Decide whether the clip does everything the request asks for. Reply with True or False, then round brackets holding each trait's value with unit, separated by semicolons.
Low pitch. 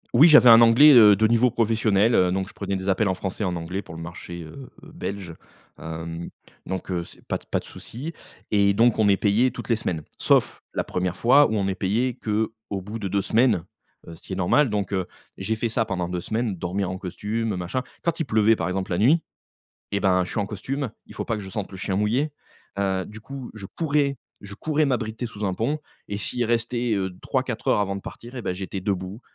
True (105 Hz)